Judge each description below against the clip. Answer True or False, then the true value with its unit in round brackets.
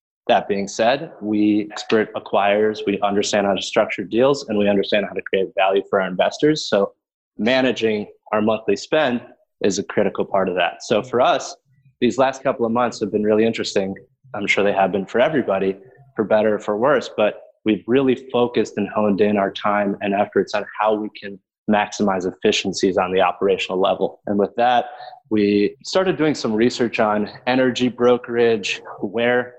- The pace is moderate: True (185 wpm)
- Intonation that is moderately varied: True (3.2 semitones)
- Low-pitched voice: True (110 Hz)